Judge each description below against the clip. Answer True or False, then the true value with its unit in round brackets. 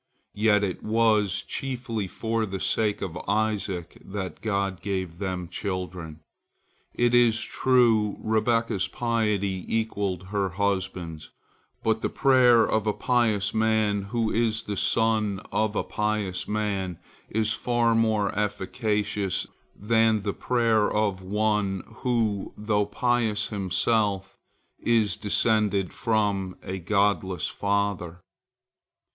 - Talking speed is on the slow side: True (115 wpm)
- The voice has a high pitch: False (105 Hz)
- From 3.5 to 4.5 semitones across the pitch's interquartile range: False (2.5 semitones)